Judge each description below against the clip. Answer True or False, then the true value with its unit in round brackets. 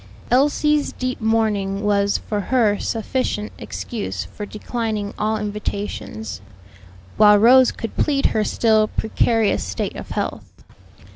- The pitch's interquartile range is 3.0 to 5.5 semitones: False (2.5 semitones)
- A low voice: False (215 Hz)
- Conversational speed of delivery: False (120 wpm)